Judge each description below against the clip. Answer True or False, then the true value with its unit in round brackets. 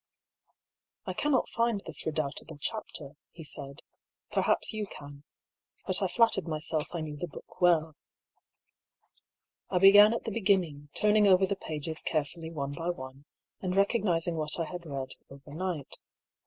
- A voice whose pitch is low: False (165 Hz)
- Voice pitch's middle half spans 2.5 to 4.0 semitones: False (4.8 semitones)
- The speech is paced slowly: False (155 wpm)